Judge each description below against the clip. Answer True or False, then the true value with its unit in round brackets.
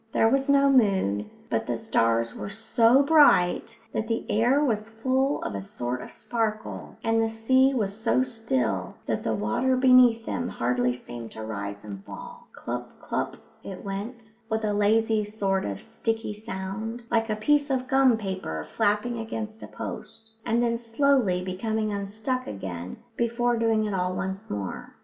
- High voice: True (220 Hz)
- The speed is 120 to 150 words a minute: False (170 wpm)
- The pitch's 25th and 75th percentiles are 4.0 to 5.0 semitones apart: True (4.6 semitones)